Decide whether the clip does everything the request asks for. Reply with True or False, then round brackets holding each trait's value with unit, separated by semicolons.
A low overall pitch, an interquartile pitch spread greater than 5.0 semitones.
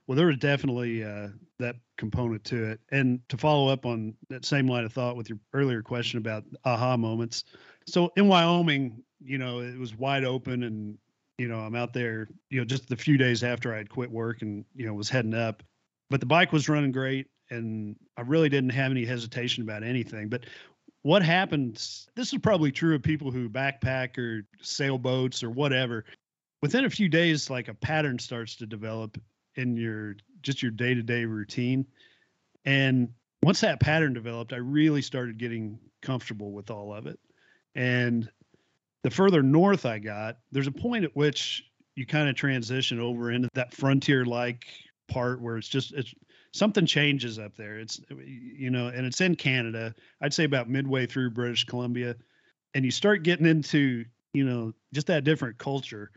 False (125 Hz; 3.2 semitones)